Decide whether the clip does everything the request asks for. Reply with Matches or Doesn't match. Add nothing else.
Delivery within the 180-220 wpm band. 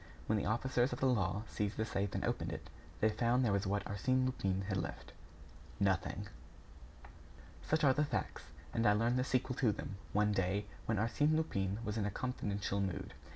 Matches